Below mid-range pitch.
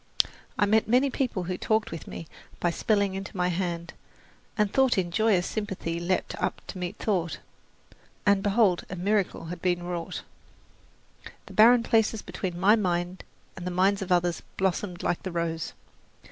No: medium, 185 Hz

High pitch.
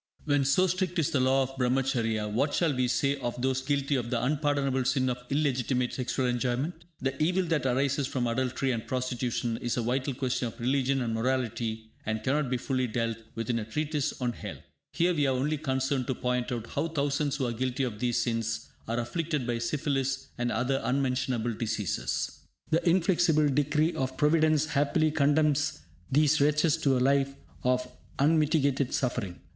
No: low, 130 Hz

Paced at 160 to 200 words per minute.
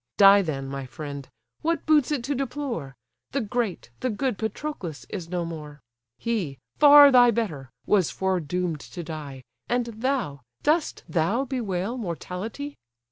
No: average, 140 wpm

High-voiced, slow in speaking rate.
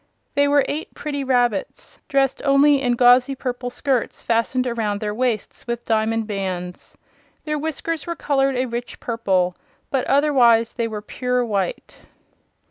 No: high, 245 Hz; average, 145 wpm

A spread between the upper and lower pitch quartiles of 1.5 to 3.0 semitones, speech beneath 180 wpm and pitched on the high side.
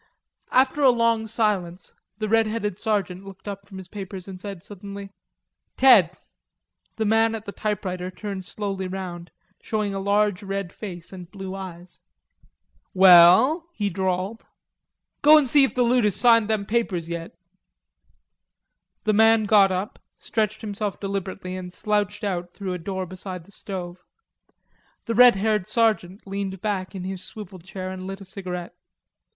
Yes: narrow, 2.6 semitones; average, 160 wpm; high, 195 Hz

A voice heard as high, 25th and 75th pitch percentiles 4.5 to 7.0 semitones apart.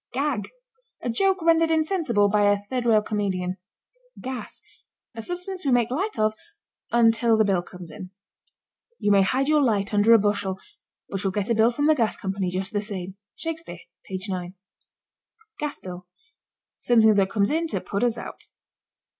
Yes: high, 220 Hz; average, 5.2 semitones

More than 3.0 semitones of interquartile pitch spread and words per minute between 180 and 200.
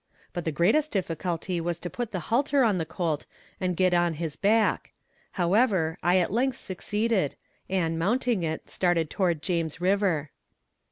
No: average, 3.9 semitones; average, 160 wpm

